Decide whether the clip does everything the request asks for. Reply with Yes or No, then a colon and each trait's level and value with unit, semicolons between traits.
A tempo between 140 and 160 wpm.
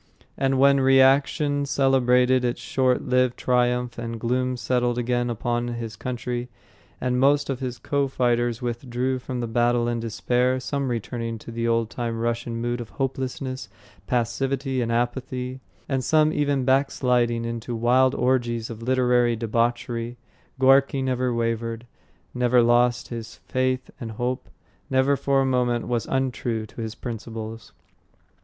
Yes: average, 145 wpm